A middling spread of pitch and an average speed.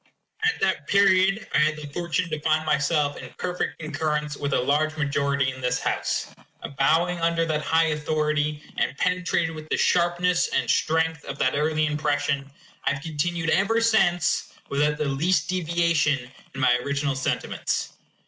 Yes: average, 3.0 semitones; average, 160 wpm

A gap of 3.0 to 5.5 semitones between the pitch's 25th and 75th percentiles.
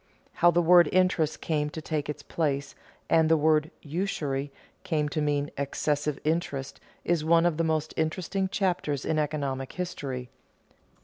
No: narrow, 2.6 semitones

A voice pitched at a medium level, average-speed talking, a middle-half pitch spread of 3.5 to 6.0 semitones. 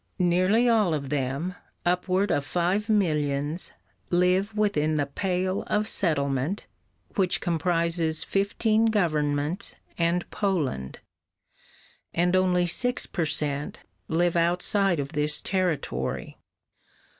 No: medium, 175 Hz; slow, 105 wpm; average, 4.3 semitones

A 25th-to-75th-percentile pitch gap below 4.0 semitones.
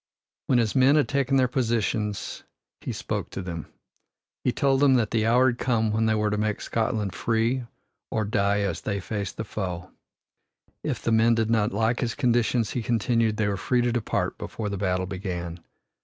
Yes: average, 3.0 semitones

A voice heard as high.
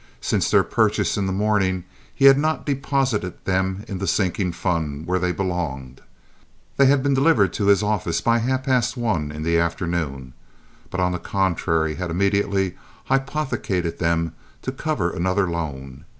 No: very low, 95 Hz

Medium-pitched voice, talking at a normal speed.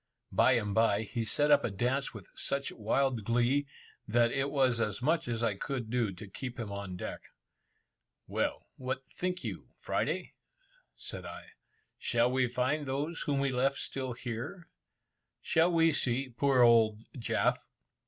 No: low, 125 Hz; average, 160 wpm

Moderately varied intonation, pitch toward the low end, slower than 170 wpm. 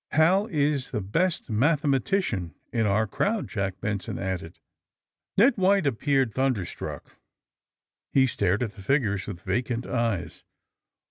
No: wide, 6.9 semitones; low, 120 Hz; average, 140 wpm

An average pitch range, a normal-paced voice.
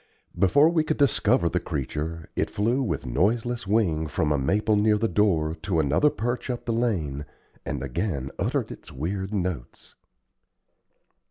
No: wide, 6.8 semitones; average, 155 wpm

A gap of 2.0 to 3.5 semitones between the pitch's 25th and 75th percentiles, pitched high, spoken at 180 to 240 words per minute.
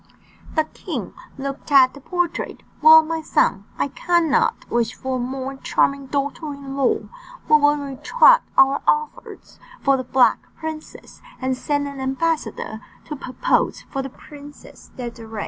No: average, 2.9 semitones; very high, 280 Hz; average, 145 wpm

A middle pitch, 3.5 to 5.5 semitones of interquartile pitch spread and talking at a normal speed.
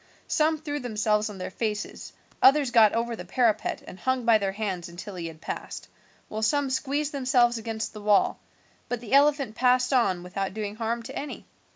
No: high, 225 Hz; average, 3.9 semitones; average, 190 wpm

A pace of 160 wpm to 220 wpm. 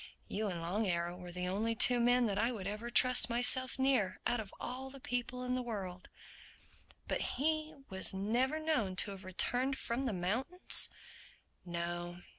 Yes: average, 170 wpm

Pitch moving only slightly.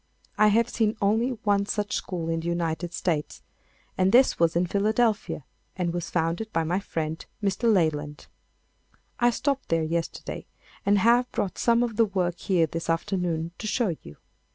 No: average, 4.6 semitones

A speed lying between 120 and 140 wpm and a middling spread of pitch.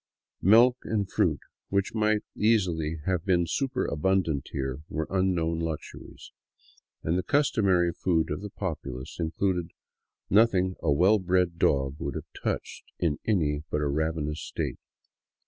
Yes: slow, 135 wpm; average, 3.8 semitones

